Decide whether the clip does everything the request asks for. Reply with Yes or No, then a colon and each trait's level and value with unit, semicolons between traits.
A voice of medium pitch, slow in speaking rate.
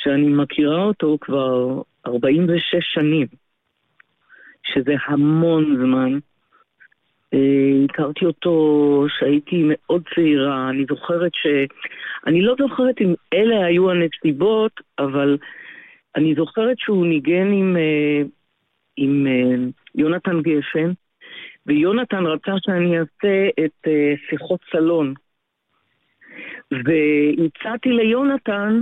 Yes: medium, 155 Hz; slow, 90 wpm